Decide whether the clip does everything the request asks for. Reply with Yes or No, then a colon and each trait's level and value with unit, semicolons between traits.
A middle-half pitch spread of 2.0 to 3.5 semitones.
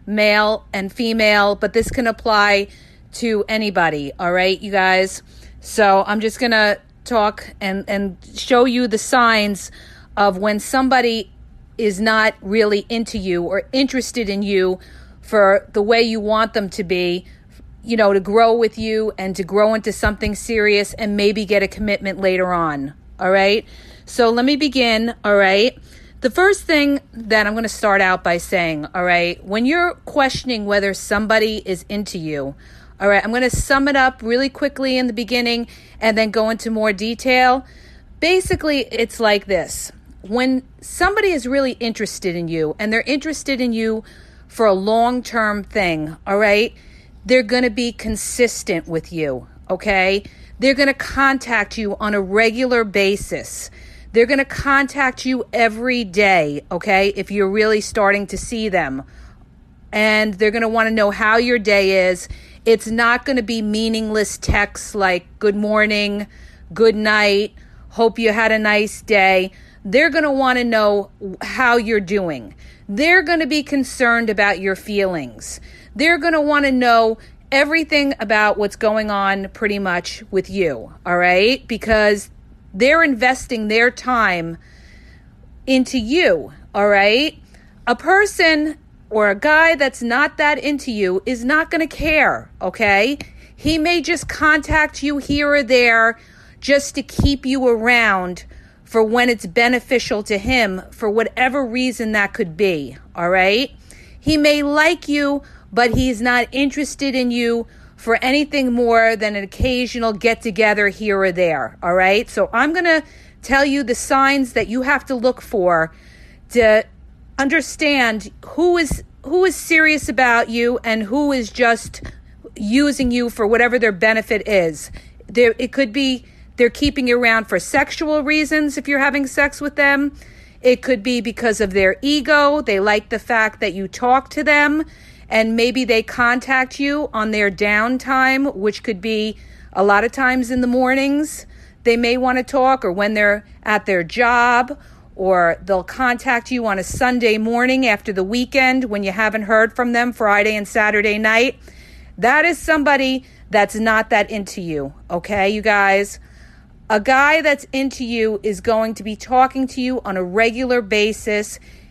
No: average, 4.0 semitones